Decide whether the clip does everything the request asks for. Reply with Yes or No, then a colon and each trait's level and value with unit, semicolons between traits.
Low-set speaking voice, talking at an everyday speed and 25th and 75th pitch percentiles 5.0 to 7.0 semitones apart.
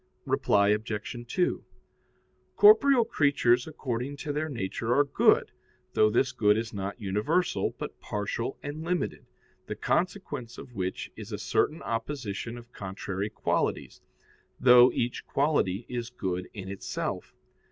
No: low, 120 Hz; slow, 130 wpm; wide, 5.6 semitones